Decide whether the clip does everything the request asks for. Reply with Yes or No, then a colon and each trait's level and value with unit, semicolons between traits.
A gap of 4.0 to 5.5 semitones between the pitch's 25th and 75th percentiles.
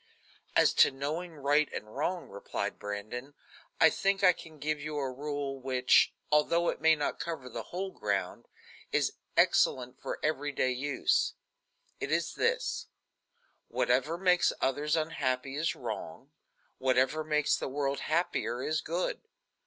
No: average, 3.5 semitones